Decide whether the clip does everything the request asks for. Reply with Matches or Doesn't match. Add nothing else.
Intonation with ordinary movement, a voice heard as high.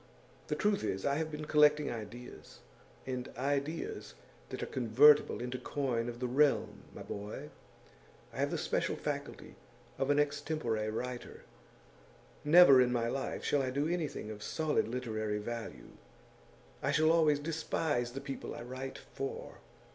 Doesn't match